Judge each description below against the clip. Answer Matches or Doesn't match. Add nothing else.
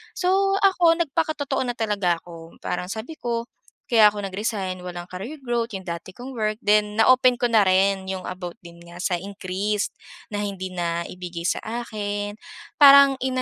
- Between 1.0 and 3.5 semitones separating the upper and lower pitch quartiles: Doesn't match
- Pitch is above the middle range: Matches